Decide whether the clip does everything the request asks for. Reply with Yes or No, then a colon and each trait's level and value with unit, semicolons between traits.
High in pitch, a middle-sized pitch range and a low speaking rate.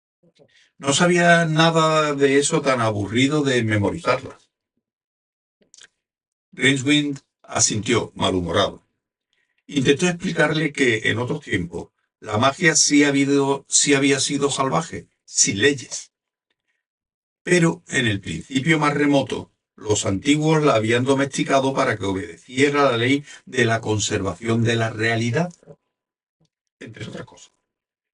No: medium, 140 Hz; average, 4.2 semitones; slow, 115 wpm